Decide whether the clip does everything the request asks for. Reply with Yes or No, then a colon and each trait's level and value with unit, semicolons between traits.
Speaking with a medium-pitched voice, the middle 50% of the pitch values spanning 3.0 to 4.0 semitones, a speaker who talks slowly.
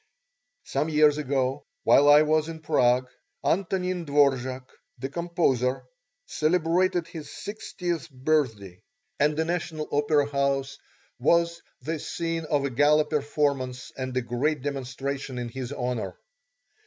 Yes: medium, 145 Hz; average, 3.6 semitones; slow, 125 wpm